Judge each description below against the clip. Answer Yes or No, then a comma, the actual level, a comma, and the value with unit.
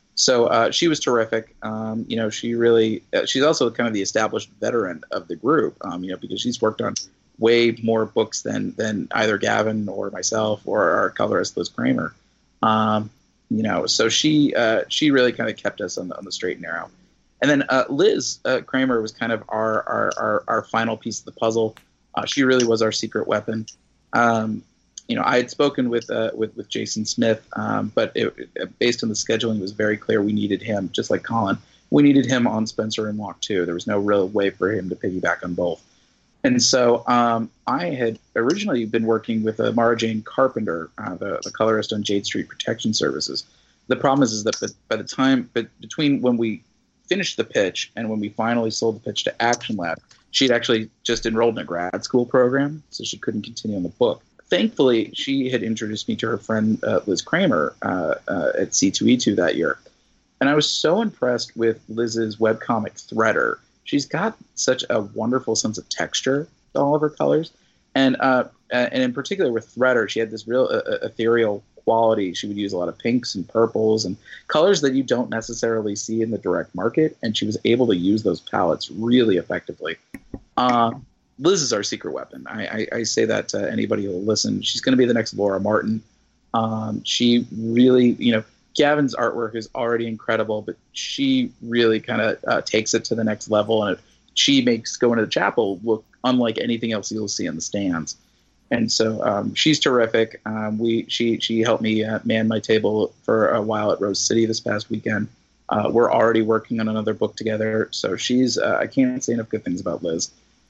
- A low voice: Yes, low, 115 Hz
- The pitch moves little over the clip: Yes, narrow, 2.0 semitones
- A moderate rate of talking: No, fast, 210 wpm